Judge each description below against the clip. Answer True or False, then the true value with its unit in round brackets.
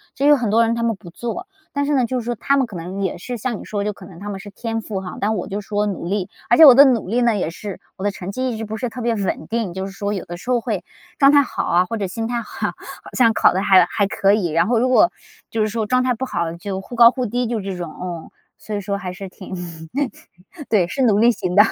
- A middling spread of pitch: True (3.9 semitones)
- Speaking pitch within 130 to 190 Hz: False (210 Hz)